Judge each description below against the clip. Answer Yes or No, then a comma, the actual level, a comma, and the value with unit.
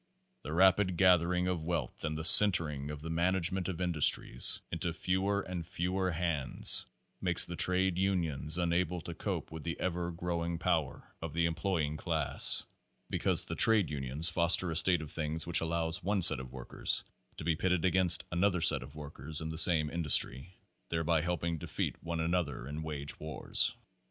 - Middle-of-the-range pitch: No, very low, 85 Hz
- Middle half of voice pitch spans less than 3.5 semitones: Yes, narrow, 2.5 semitones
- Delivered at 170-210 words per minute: Yes, average, 175 wpm